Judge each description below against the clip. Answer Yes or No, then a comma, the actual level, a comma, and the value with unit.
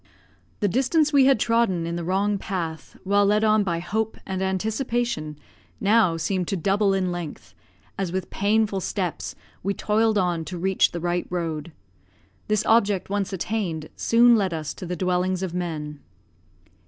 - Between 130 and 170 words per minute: Yes, average, 165 wpm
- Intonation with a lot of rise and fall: No, average, 3.5 semitones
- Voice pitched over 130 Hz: Yes, high, 190 Hz